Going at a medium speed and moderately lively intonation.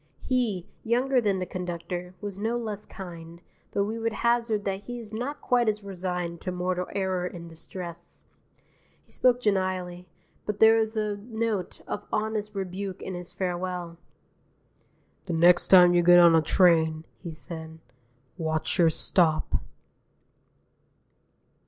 Yes: average, 145 wpm; average, 3.5 semitones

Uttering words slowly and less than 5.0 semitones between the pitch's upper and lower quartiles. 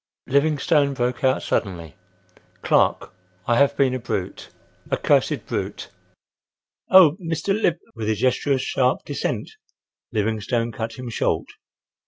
Yes: slow, 130 wpm; average, 4.1 semitones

